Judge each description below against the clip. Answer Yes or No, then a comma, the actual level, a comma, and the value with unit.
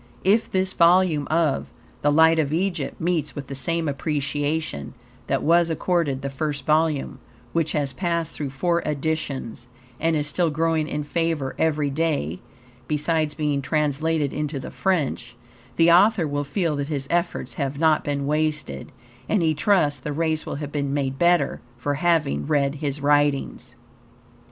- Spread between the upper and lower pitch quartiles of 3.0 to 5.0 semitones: No, narrow, 2.6 semitones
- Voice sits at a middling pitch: Yes, medium, 150 Hz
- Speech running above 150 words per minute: Yes, average, 160 wpm